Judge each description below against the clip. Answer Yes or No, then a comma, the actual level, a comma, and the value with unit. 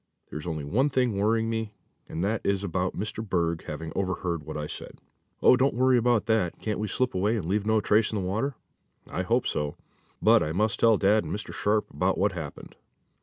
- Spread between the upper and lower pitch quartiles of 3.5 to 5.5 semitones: Yes, average, 3.9 semitones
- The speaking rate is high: Yes, fast, 215 wpm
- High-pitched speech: No, low, 105 Hz